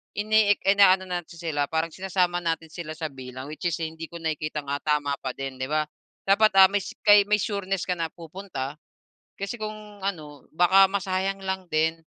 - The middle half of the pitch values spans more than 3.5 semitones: Yes, average, 4.1 semitones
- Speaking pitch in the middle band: Yes, medium, 175 Hz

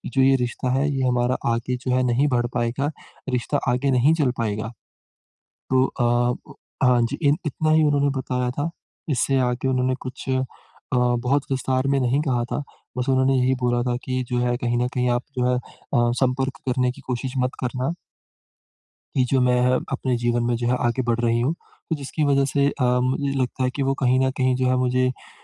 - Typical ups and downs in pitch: No, narrow, 1.5 semitones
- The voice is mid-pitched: No, low, 130 Hz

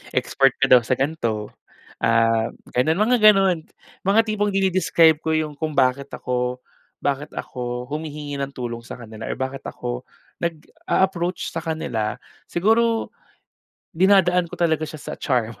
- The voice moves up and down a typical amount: No, wide, 6.1 semitones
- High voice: No, medium, 150 Hz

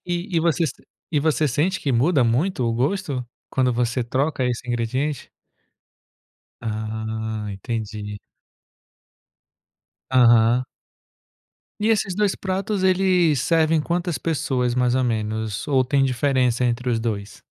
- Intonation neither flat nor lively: No, wide, 5.8 semitones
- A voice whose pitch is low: Yes, low, 130 Hz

